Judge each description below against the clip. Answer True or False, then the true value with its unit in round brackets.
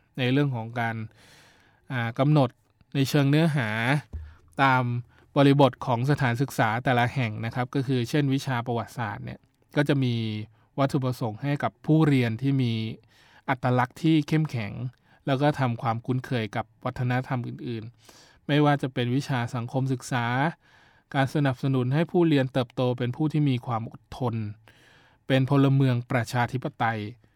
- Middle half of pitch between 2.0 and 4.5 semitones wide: True (3.0 semitones)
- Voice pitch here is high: False (125 Hz)